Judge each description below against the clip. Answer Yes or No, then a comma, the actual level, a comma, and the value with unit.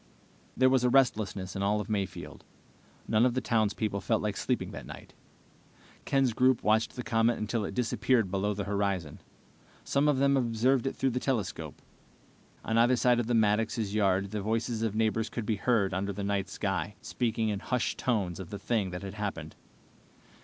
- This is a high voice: No, low, 110 Hz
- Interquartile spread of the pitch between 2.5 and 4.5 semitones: Yes, average, 3.3 semitones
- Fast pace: No, average, 190 wpm